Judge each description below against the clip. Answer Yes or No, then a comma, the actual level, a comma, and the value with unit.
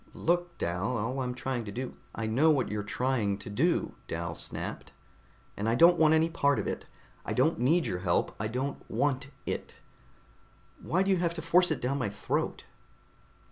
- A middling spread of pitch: No, wide, 6.3 semitones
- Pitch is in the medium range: No, low, 130 Hz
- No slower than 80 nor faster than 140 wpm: No, average, 195 wpm